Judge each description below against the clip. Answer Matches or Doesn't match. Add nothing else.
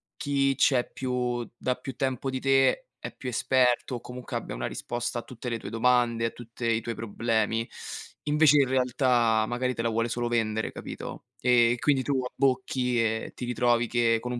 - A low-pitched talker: Matches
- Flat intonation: Matches